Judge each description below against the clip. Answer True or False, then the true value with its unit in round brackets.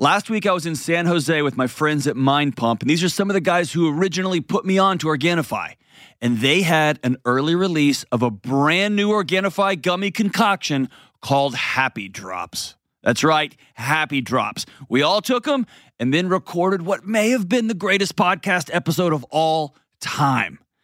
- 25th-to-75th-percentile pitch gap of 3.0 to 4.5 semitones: False (5.6 semitones)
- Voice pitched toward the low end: False (165 Hz)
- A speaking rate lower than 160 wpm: False (185 wpm)